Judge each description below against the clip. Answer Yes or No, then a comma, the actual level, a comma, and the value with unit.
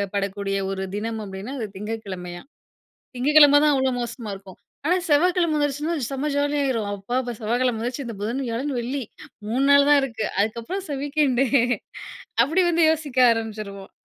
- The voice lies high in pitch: Yes, high, 245 Hz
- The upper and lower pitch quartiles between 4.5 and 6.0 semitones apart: Yes, average, 5.1 semitones